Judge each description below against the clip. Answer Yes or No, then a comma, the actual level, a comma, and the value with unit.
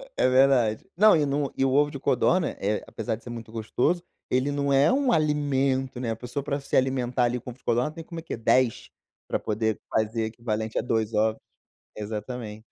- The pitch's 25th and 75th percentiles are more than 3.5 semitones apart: Yes, average, 4.1 semitones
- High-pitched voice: No, low, 125 Hz